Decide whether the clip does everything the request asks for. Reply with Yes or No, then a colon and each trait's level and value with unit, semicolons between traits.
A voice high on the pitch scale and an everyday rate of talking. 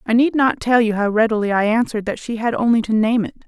No: high, 225 Hz; fast, 275 wpm